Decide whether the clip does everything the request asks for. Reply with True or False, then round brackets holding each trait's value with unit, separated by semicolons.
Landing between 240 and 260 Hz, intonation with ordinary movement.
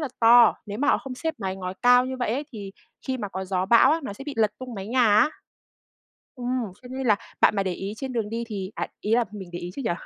False (230 Hz; 4.4 semitones)